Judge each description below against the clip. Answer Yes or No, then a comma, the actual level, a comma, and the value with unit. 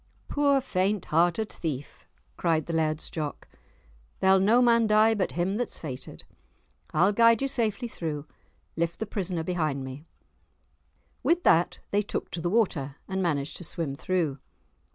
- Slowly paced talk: No, average, 155 wpm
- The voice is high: No, medium, 180 Hz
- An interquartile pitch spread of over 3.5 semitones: Yes, wide, 5.4 semitones